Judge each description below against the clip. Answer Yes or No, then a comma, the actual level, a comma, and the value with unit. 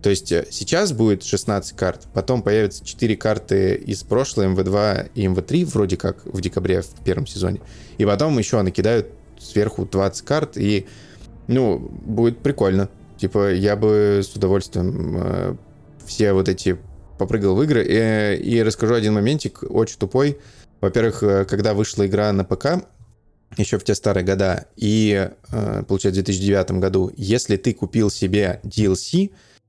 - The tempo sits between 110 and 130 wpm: No, average, 150 wpm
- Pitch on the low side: Yes, low, 105 Hz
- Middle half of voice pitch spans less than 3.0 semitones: Yes, narrow, 2.5 semitones